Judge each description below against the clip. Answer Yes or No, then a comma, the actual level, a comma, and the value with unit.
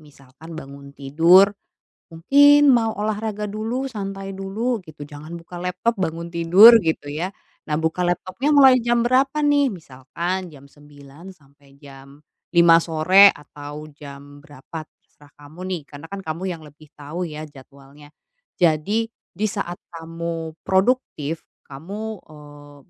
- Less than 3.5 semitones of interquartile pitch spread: No, average, 5.3 semitones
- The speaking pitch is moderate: Yes, medium, 165 Hz